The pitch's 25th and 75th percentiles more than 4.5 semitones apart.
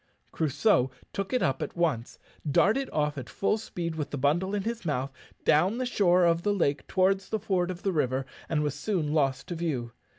Yes: average, 5.2 semitones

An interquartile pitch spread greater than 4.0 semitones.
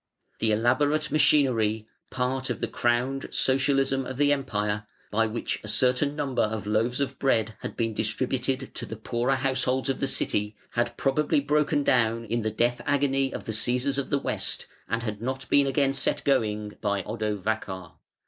No: average, 3.7 semitones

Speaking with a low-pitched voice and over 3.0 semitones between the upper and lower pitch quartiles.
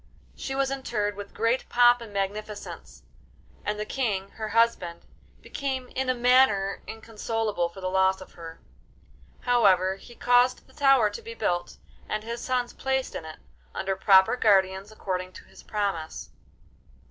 No: high, 215 Hz; average, 4.5 semitones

